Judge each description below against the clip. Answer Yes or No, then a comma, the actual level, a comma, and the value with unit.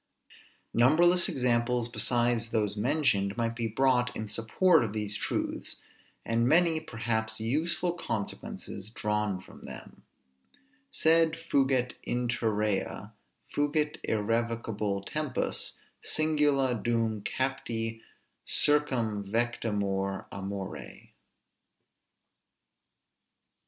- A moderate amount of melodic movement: Yes, average, 4.2 semitones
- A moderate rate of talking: No, slow, 80 wpm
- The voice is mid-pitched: No, low, 115 Hz